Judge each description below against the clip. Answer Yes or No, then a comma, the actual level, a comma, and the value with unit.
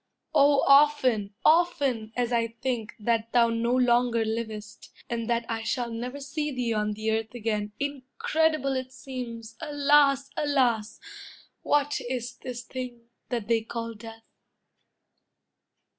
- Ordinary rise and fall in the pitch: Yes, average, 3.2 semitones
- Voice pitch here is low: No, high, 240 Hz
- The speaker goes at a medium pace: No, slow, 130 wpm